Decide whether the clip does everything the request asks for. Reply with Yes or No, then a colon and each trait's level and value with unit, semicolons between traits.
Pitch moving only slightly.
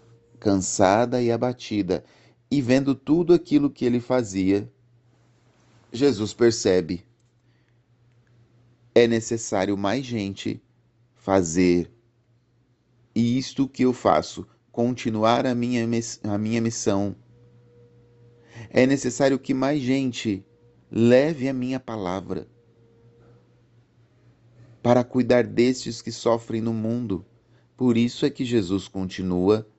Yes: narrow, 1.4 semitones